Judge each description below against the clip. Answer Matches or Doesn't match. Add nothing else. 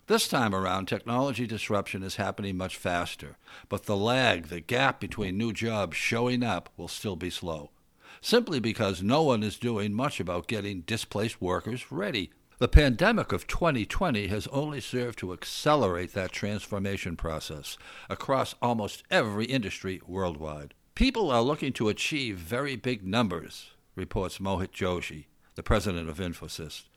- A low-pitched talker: Matches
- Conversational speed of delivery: Matches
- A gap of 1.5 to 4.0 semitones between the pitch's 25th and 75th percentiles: Doesn't match